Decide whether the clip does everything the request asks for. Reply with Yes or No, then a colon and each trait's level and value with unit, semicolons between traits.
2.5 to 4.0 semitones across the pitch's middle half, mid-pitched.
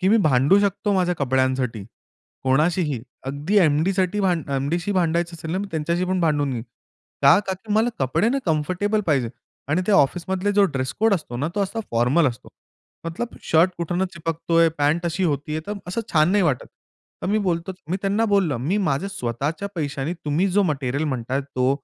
No: average, 5.2 semitones; medium, 165 Hz